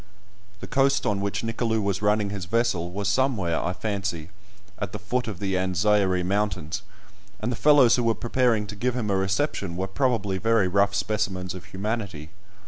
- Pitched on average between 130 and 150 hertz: No, low, 100 Hz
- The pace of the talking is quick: No, average, 180 wpm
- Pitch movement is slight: No, average, 3.3 semitones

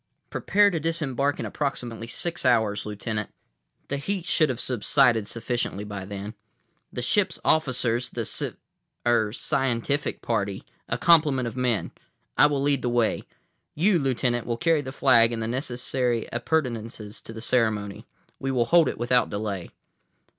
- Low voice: Yes, low, 125 Hz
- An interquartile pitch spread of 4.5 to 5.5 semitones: No, average, 4.0 semitones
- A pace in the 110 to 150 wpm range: Yes, average, 145 wpm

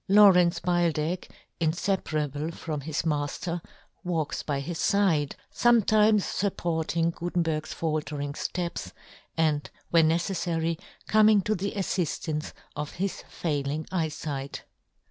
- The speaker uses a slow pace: Yes, slow, 110 wpm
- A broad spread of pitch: No, average, 3.0 semitones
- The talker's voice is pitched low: No, medium, 165 Hz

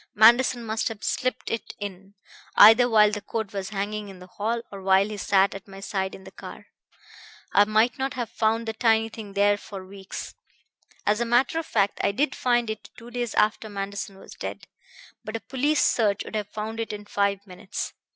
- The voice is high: Yes, high, 215 Hz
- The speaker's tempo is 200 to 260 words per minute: Yes, fast, 205 wpm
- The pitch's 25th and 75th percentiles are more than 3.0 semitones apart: No, narrow, 2.4 semitones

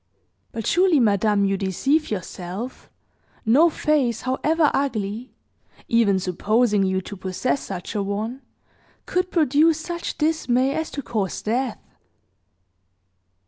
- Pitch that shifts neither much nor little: No, wide, 6.7 semitones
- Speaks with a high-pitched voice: Yes, high, 235 Hz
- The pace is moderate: No, slow, 115 wpm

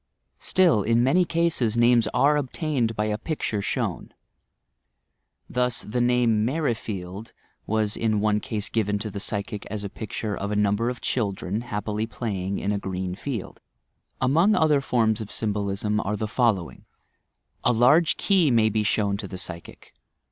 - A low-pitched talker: Yes, low, 110 Hz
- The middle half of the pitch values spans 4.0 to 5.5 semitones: No, average, 3.2 semitones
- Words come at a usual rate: Yes, average, 160 wpm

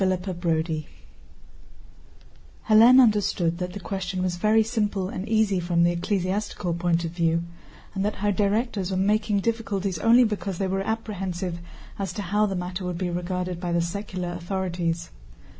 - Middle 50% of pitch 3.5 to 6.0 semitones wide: No, average, 2.9 semitones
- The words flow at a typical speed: Yes, average, 160 wpm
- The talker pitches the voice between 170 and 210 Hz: Yes, medium, 185 Hz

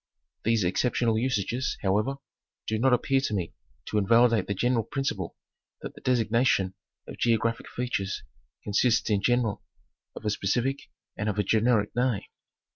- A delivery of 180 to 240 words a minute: No, average, 145 wpm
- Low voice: Yes, low, 115 Hz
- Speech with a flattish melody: No, average, 3.2 semitones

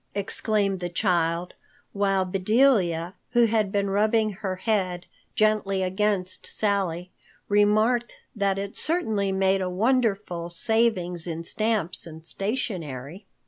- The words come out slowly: Yes, slow, 115 wpm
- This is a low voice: No, high, 195 Hz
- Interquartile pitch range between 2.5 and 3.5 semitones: Yes, average, 3.1 semitones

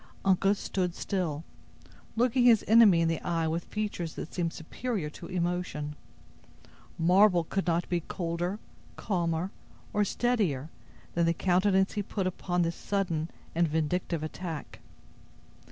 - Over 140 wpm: No, slow, 135 wpm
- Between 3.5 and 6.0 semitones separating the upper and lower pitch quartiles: No, average, 2.9 semitones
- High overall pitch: No, medium, 175 Hz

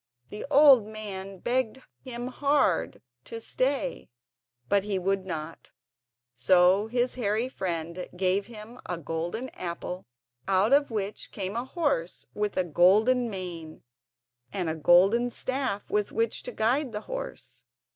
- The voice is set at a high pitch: Yes, high, 210 Hz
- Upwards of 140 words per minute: No, slow, 135 wpm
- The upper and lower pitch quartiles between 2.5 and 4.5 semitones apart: No, average, 5.1 semitones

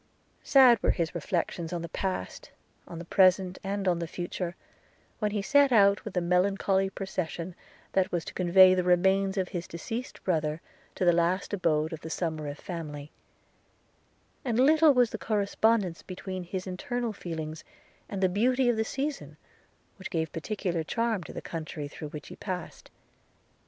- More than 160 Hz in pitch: Yes, medium, 185 Hz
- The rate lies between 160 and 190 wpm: Yes, average, 165 wpm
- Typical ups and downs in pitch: Yes, average, 3.3 semitones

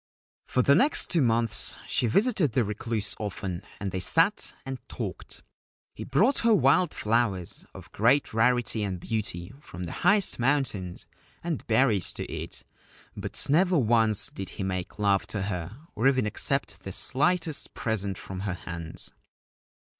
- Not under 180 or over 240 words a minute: No, average, 155 wpm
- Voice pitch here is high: No, low, 110 Hz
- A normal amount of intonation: No, wide, 6.0 semitones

